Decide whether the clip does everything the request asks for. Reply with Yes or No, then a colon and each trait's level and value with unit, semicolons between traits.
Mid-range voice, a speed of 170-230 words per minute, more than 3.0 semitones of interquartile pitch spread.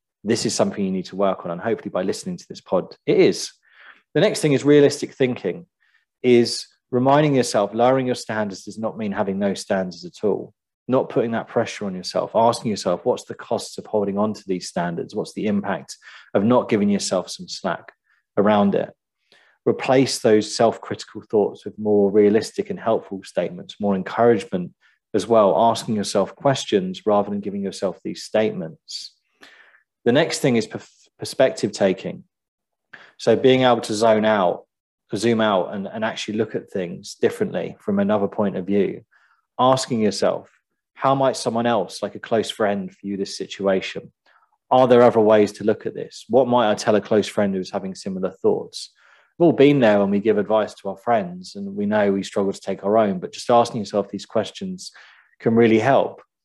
No: low, 110 Hz; average, 190 wpm; average, 4.4 semitones